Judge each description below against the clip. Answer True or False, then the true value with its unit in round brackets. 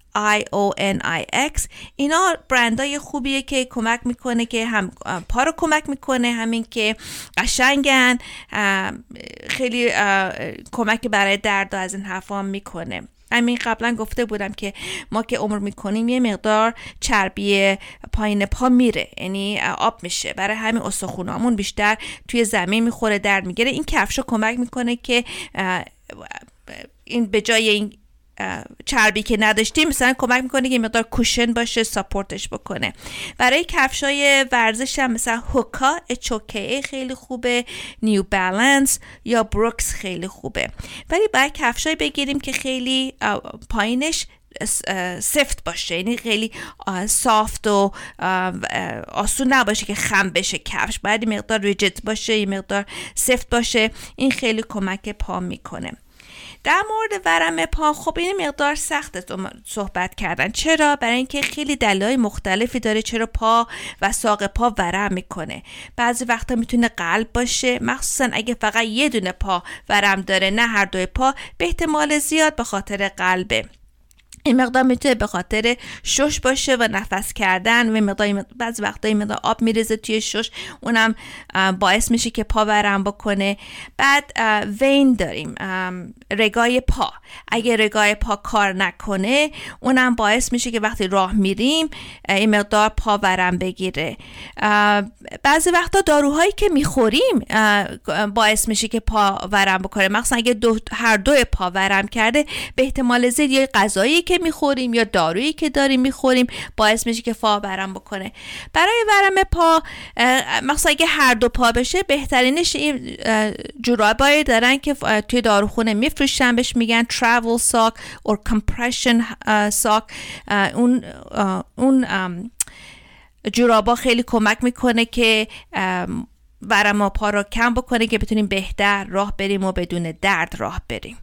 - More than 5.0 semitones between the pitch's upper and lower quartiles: False (3.9 semitones)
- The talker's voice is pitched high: True (230 Hz)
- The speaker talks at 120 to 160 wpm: True (140 wpm)